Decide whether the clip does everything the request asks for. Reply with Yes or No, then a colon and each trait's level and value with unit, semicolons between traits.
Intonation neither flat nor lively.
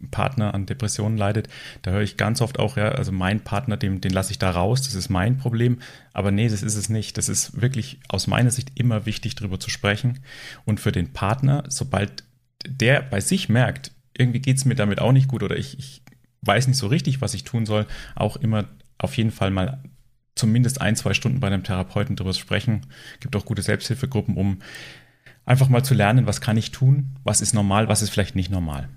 Yes: average, 3.8 semitones